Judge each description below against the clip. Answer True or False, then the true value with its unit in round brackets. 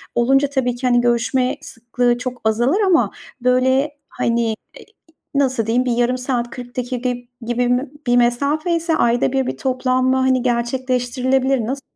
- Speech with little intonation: True (1.6 semitones)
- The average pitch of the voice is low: False (250 Hz)